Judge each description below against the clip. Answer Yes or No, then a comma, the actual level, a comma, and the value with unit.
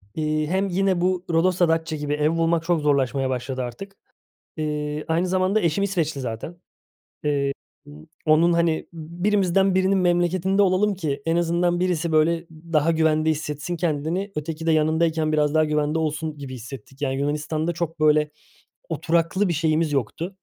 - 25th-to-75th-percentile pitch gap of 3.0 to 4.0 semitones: No, narrow, 2.6 semitones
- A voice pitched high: No, medium, 160 Hz